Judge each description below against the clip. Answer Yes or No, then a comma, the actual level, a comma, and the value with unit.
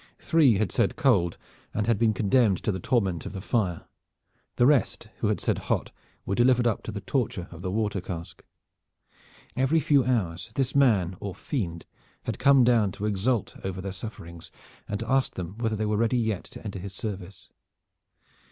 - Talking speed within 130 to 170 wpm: No, average, 190 wpm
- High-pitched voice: No, low, 105 Hz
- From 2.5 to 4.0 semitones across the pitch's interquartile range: No, average, 4.4 semitones